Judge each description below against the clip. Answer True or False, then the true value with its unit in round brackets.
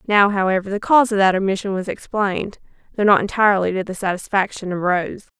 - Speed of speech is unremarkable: True (190 wpm)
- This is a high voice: True (195 Hz)